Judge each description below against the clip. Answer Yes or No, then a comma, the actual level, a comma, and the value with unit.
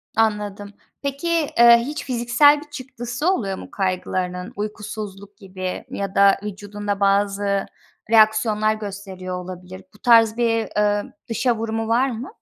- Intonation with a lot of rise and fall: No, average, 3.2 semitones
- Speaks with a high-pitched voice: Yes, high, 215 Hz